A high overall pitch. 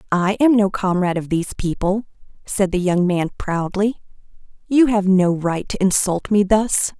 Yes: high, 195 Hz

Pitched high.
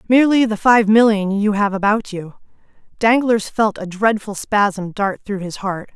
Yes: high, 210 Hz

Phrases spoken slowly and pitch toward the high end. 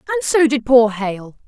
No: fast, 205 wpm; very high, 255 Hz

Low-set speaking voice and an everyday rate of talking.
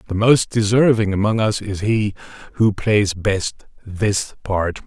Yes: low, 105 Hz; average, 150 wpm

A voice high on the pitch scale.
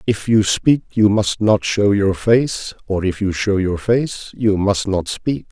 No: low, 105 Hz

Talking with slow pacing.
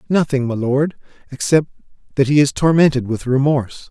No: average, 155 wpm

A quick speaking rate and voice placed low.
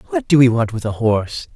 Yes: fast, 270 wpm; low, 130 Hz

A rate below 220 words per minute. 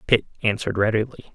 Yes: slow, 135 wpm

